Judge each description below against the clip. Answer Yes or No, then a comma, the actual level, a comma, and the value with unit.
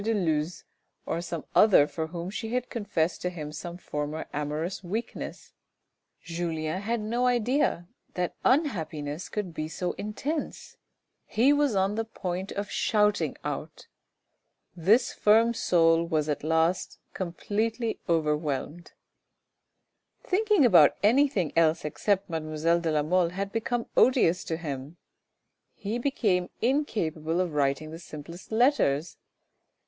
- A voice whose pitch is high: No, medium, 180 Hz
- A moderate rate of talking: No, slow, 130 wpm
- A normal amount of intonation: No, wide, 5.7 semitones